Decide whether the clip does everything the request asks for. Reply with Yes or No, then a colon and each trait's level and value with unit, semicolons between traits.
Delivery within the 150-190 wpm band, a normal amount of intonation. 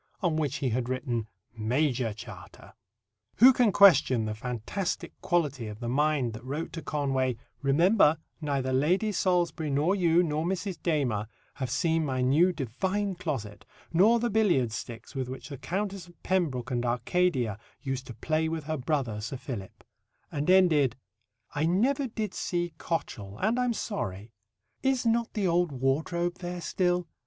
No: average, 160 wpm; wide, 6.0 semitones